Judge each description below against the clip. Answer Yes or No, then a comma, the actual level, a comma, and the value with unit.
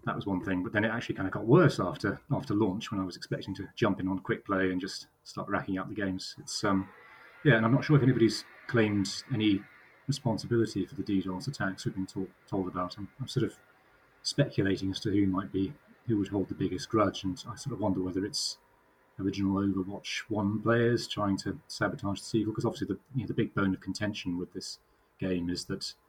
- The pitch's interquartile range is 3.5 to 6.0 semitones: No, average, 2.8 semitones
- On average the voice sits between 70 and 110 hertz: Yes, low, 100 Hz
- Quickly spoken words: Yes, fast, 230 wpm